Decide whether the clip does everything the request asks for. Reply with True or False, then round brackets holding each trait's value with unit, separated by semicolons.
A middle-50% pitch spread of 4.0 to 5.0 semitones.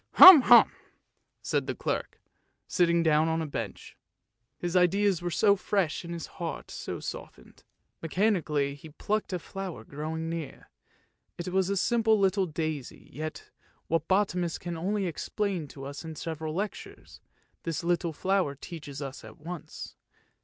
False (3.6 semitones)